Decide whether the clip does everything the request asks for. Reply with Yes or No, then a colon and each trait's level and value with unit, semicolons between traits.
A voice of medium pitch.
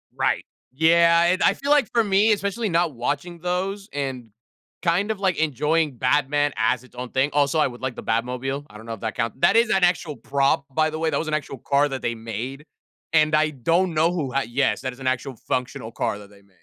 Yes: medium, 145 Hz